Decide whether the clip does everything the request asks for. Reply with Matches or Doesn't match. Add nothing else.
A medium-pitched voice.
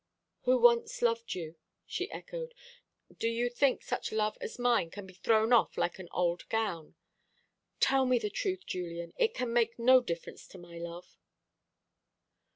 Doesn't match